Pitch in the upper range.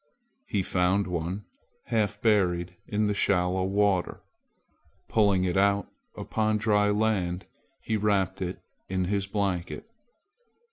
No: low, 100 Hz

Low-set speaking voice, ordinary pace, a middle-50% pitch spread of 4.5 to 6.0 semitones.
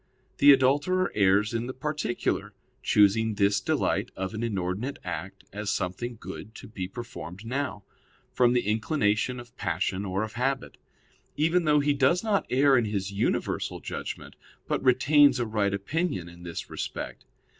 Yes: low, 115 Hz; average, 155 wpm; wide, 5.4 semitones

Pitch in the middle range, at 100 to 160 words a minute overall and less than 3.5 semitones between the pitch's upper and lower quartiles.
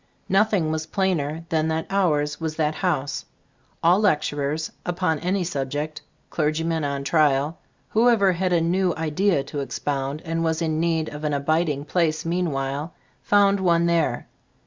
Yes: medium, 160 Hz; average, 155 wpm; average, 3.0 semitones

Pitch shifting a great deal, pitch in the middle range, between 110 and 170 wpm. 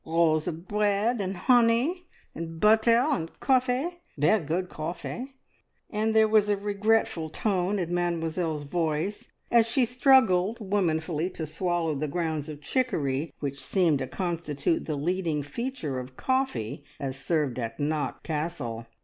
Yes: wide, 6.1 semitones; medium, 175 Hz; average, 140 wpm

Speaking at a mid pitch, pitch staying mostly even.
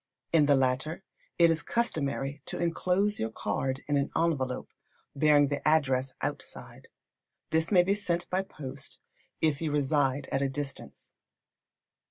No: medium, 145 Hz; average, 3.6 semitones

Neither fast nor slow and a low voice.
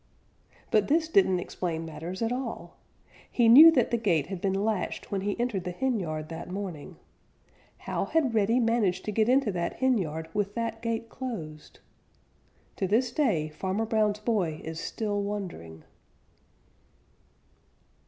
No: average, 145 wpm; high, 205 Hz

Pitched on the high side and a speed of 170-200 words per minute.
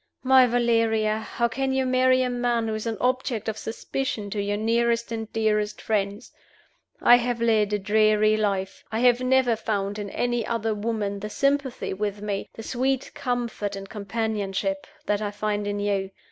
Yes: high, 220 Hz; average, 175 wpm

